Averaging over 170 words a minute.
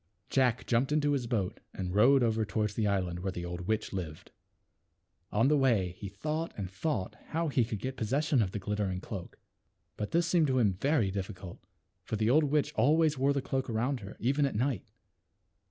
Yes: average, 200 wpm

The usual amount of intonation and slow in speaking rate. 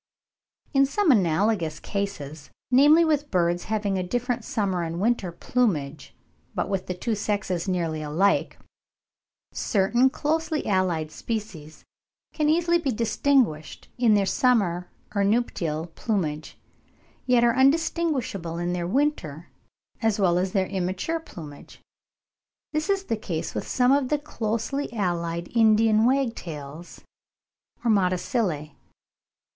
No: wide, 6.4 semitones; slow, 125 wpm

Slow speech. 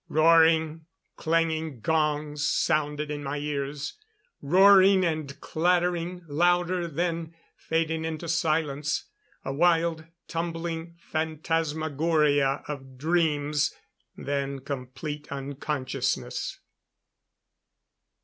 Yes: slow, 80 wpm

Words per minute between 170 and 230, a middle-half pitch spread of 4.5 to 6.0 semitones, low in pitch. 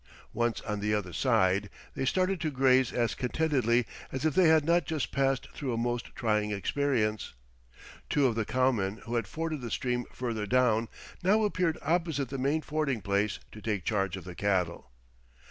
Yes: average, 180 wpm; wide, 5.4 semitones; low, 125 Hz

